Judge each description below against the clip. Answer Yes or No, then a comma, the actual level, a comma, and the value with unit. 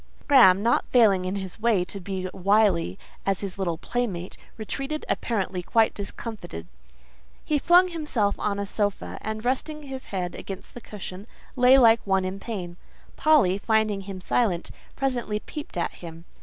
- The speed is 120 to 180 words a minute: Yes, average, 155 wpm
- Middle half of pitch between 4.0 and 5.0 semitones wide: Yes, average, 4.6 semitones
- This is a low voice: No, high, 205 Hz